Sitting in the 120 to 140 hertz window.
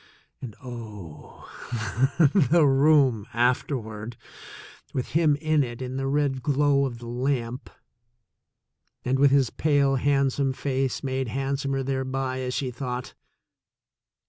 Yes: low, 135 Hz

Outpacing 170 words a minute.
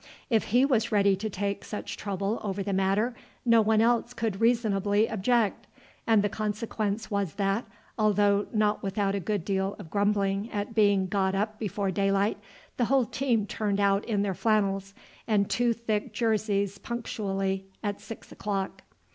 No: average, 165 wpm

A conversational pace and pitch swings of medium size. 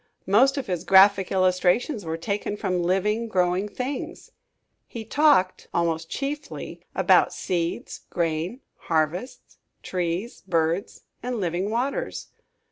No: slow, 115 wpm; average, 5.0 semitones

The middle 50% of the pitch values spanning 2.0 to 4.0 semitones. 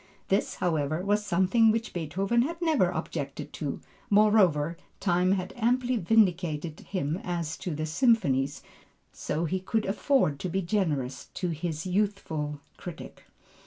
No: average, 5.1 semitones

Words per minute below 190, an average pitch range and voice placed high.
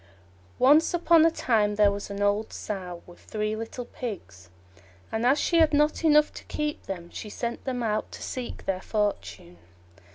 No: average, 175 wpm; wide, 6.1 semitones; high, 220 Hz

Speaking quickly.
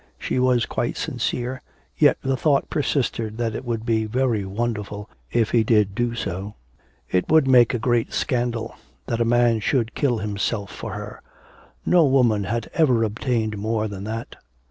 No: average, 165 wpm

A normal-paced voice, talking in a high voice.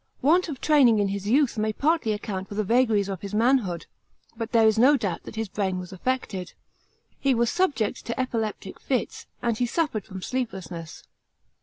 Yes: average, 185 wpm; high, 220 Hz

